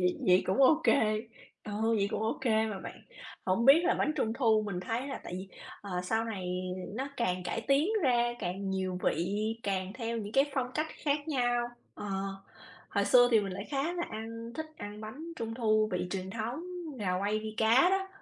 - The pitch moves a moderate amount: Yes, average, 4.5 semitones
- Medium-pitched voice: No, high, 225 Hz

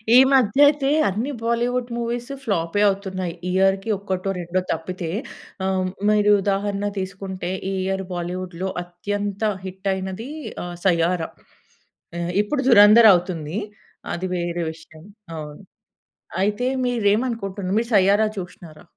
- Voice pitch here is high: Yes, high, 195 Hz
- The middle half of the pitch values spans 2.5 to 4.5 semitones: Yes, average, 2.9 semitones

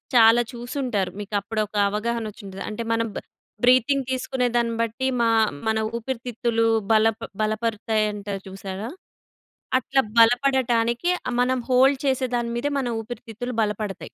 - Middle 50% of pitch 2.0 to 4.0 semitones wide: Yes, narrow, 2.6 semitones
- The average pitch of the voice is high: Yes, high, 230 Hz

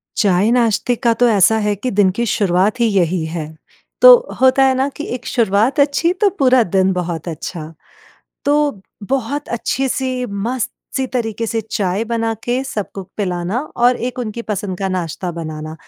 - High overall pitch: Yes, high, 220 Hz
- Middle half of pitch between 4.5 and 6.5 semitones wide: Yes, average, 5.1 semitones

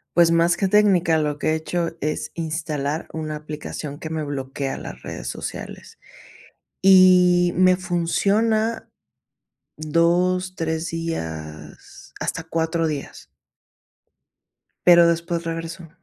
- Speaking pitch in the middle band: Yes, medium, 165 Hz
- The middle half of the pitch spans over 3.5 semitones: No, narrow, 2.5 semitones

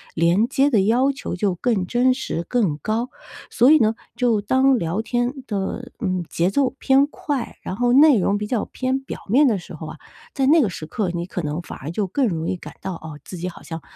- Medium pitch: No, high, 220 Hz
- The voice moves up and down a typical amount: No, wide, 6.2 semitones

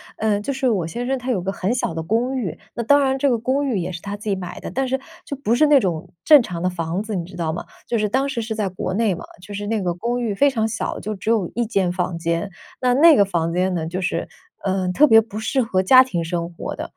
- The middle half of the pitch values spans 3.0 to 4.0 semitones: No, average, 5.3 semitones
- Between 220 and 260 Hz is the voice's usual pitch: No, high, 210 Hz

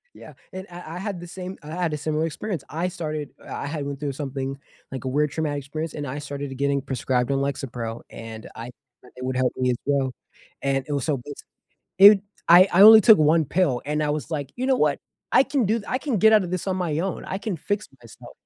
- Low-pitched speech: No, medium, 150 Hz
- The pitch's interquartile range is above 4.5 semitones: Yes, average, 5.0 semitones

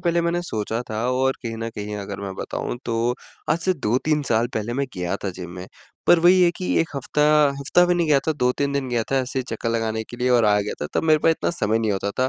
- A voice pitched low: Yes, low, 120 Hz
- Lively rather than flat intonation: Yes, wide, 5.9 semitones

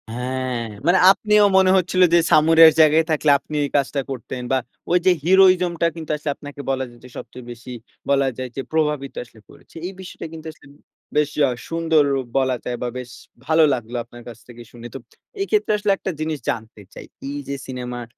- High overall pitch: No, medium, 145 Hz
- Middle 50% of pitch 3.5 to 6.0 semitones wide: Yes, average, 4.6 semitones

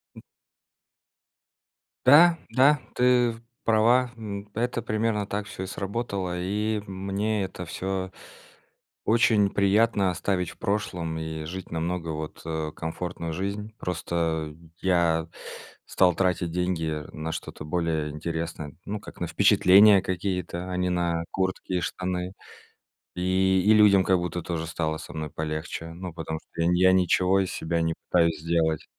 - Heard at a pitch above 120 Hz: No, very low, 90 Hz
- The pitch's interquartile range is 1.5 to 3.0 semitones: No, average, 3.4 semitones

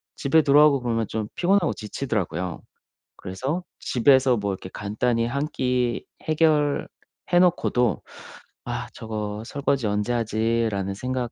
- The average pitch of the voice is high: No, low, 120 Hz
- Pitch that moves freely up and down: No, average, 4.7 semitones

